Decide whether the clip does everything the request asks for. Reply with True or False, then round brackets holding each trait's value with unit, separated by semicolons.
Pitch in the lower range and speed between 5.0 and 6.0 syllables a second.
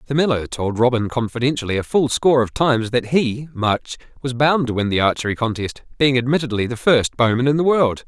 True (125 Hz; 5.8 syllables/s)